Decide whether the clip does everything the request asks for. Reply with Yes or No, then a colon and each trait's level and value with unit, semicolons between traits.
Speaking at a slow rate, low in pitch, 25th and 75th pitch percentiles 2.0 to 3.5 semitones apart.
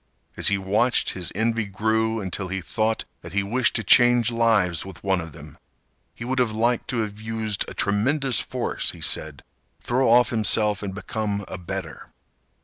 No: average, 180 wpm; low, 110 Hz; average, 2.9 semitones